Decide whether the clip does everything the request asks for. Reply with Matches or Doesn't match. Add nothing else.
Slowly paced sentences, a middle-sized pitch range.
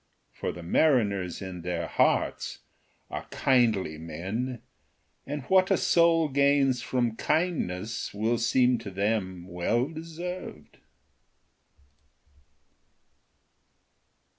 Doesn't match